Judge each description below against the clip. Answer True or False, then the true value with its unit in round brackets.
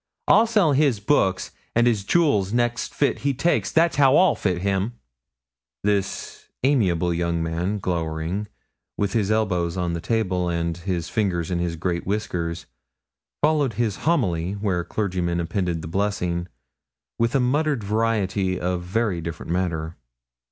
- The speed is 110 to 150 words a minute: True (145 wpm)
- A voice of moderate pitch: False (95 Hz)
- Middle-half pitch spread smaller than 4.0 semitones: False (5.1 semitones)